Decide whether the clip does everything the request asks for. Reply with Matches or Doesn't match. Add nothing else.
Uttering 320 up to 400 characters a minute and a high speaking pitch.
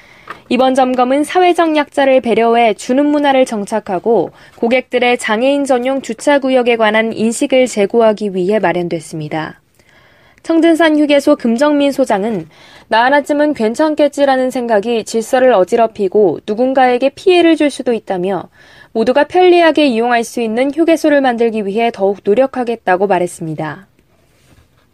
Matches